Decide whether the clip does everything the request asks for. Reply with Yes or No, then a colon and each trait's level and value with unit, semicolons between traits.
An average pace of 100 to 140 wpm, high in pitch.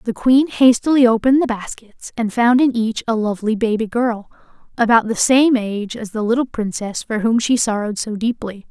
No: average, 195 wpm; high, 230 Hz